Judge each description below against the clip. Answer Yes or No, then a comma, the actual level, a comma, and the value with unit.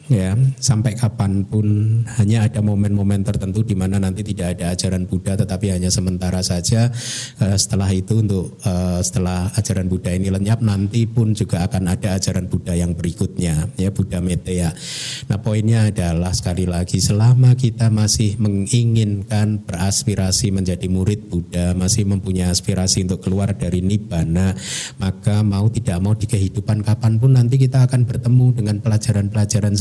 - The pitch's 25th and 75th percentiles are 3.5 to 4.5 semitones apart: No, average, 3.0 semitones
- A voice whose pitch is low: Yes, low, 100 Hz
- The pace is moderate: No, fast, 145 wpm